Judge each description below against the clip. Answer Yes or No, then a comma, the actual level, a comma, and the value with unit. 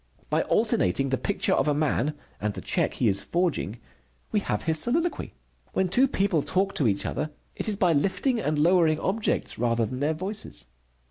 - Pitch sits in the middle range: Yes, medium, 160 Hz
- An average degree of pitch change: No, wide, 6.8 semitones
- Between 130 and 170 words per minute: No, average, 190 wpm